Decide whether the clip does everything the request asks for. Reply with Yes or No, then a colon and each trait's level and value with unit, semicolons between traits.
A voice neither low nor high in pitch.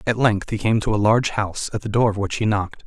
No: low, 105 Hz